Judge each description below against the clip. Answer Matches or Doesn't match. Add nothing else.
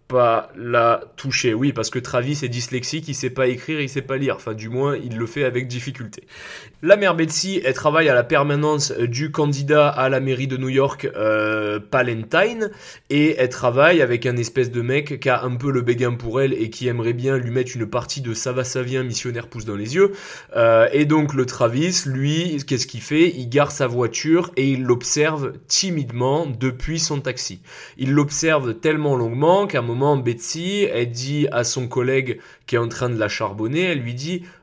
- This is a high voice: Doesn't match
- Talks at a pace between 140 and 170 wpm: Doesn't match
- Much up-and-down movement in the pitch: Doesn't match